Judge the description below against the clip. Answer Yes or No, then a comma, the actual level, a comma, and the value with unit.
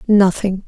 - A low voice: No, high, 195 Hz